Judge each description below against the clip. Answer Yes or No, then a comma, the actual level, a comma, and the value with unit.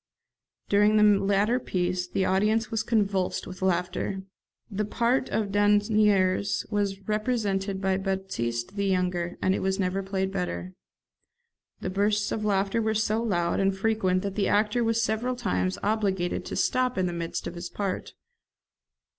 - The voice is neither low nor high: No, high, 195 Hz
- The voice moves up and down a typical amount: No, narrow, 2.3 semitones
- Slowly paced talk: No, average, 155 wpm